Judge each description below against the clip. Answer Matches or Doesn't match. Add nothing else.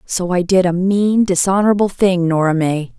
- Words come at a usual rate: Matches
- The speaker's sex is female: Matches